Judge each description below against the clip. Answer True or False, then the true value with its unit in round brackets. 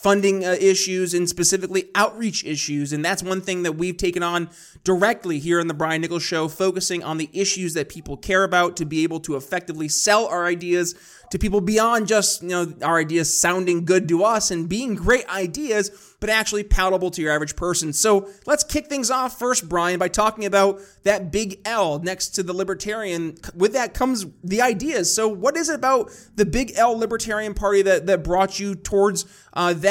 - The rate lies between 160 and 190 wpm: False (200 wpm)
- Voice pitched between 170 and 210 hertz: True (190 Hz)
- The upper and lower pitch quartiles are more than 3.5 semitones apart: False (3.2 semitones)